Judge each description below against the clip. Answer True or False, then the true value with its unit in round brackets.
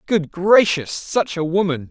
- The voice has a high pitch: False (180 Hz)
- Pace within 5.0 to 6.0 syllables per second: False (4.0 syllables/s)